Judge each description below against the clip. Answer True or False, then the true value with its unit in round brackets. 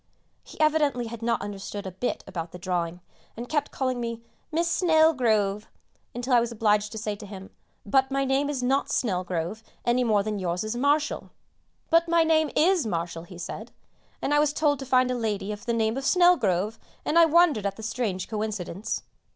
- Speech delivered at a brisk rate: False (195 wpm)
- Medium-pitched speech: False (230 Hz)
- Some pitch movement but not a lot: False (5.8 semitones)